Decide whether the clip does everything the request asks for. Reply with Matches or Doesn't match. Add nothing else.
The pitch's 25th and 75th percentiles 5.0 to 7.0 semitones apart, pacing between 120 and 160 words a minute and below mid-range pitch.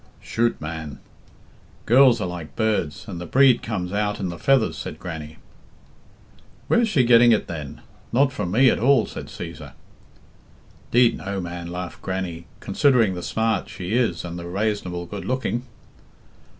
Matches